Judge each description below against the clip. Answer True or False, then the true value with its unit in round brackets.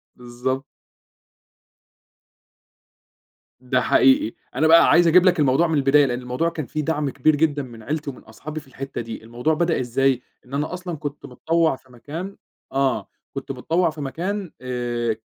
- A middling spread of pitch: True (4.2 semitones)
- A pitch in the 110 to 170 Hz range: True (140 Hz)